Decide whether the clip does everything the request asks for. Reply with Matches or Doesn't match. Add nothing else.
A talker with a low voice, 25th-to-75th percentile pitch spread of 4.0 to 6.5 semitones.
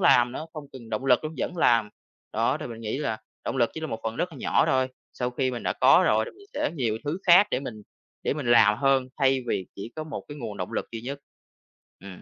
Matches